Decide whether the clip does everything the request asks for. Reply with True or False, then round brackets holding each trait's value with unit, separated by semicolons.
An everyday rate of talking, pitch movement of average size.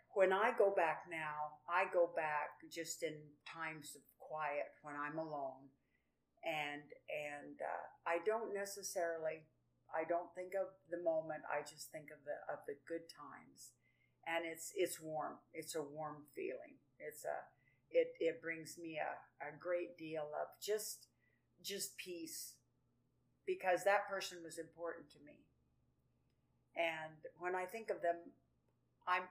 True (150 wpm; 3.3 semitones)